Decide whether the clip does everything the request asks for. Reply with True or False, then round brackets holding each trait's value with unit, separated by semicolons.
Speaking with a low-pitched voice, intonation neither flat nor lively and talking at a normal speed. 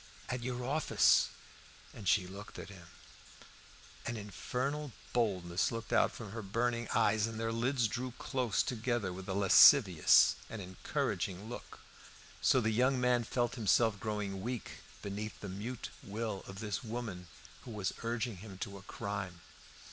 True (110 Hz; 3.5 semitones; 155 wpm)